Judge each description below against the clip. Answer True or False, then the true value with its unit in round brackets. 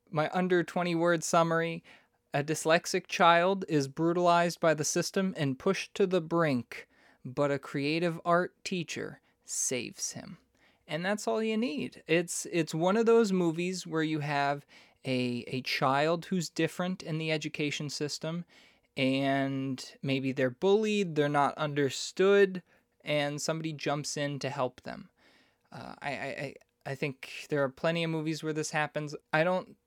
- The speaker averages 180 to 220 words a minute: False (155 wpm)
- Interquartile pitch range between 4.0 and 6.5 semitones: False (3.5 semitones)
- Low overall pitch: False (160 Hz)